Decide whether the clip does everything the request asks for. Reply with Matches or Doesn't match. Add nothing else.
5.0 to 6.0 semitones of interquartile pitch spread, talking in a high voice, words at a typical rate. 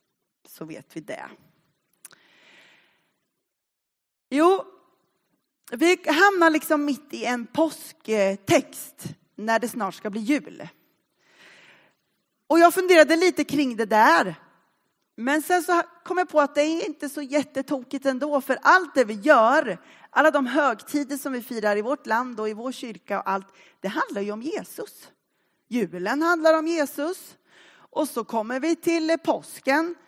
Matches